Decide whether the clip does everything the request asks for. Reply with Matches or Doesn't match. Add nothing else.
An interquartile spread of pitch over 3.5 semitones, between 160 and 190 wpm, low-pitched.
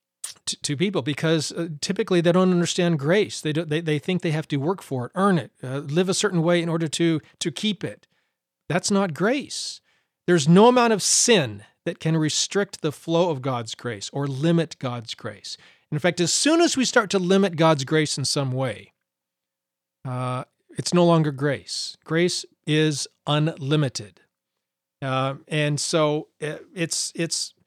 Doesn't match